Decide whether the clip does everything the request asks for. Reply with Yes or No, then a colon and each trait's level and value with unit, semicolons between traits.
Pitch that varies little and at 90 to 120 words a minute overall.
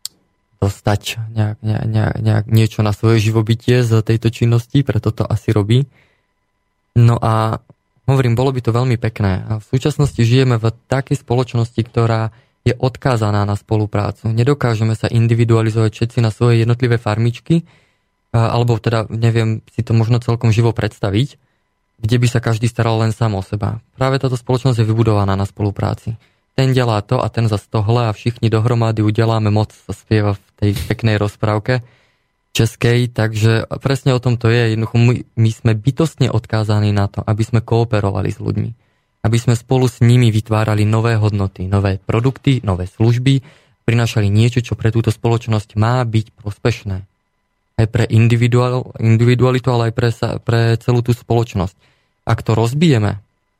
No: narrow, 2.0 semitones; average, 155 wpm